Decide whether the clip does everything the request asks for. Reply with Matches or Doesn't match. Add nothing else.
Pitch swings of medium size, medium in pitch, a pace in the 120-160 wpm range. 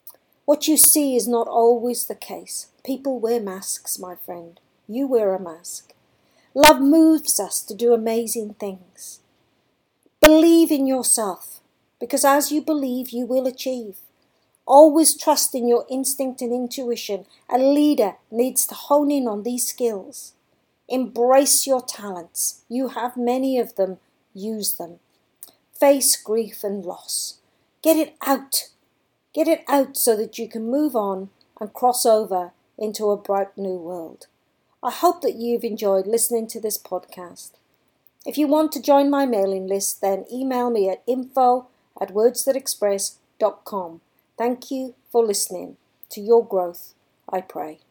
Doesn't match